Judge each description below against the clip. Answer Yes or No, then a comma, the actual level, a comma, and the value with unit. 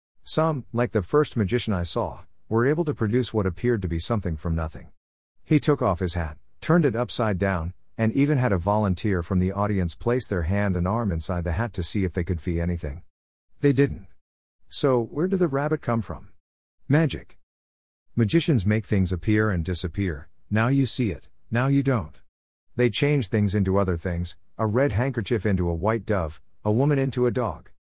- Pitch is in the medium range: No, low, 100 Hz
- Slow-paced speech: No, average, 195 wpm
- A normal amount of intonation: No, wide, 5.9 semitones